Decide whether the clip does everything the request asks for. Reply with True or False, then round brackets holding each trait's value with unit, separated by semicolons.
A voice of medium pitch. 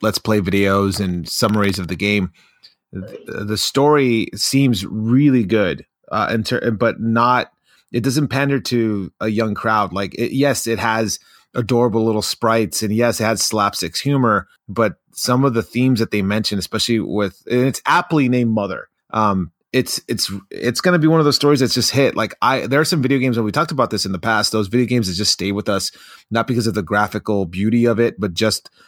False (115 Hz)